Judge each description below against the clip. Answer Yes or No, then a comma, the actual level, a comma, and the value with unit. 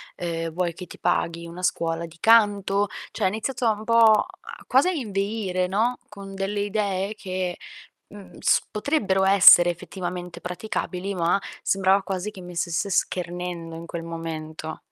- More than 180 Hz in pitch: Yes, high, 190 Hz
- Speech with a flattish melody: No, average, 3.0 semitones